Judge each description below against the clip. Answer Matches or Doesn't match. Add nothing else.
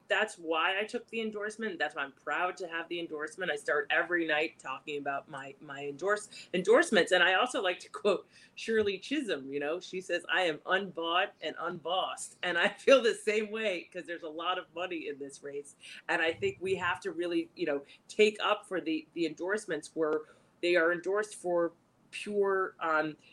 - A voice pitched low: Doesn't match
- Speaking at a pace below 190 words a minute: Doesn't match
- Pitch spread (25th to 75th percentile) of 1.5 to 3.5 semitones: Doesn't match